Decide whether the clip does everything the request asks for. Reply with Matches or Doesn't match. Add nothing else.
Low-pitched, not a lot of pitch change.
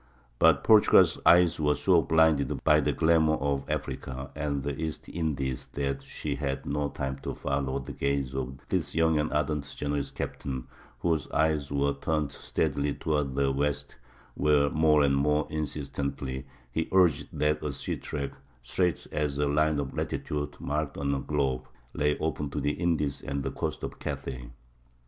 Matches